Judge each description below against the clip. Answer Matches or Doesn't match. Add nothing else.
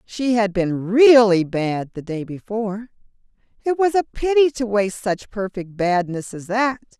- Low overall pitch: Doesn't match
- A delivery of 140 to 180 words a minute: Matches